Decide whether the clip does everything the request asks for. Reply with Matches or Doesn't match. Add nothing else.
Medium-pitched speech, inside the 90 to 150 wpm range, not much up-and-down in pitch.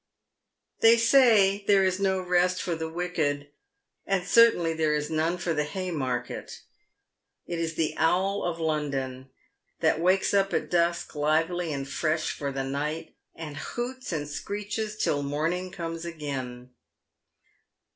Doesn't match